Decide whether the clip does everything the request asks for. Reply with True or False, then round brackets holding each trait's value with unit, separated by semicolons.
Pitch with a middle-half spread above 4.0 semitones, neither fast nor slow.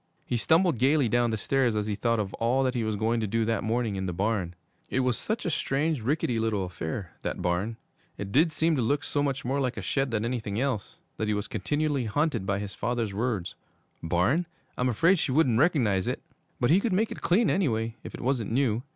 False (4.8 semitones; 230 wpm)